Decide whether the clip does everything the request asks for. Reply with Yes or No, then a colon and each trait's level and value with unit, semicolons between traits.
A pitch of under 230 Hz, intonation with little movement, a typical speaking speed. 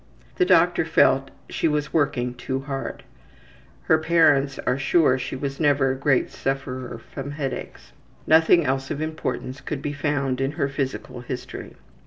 Yes: low, 135 Hz; narrow, 2.0 semitones; average, 155 wpm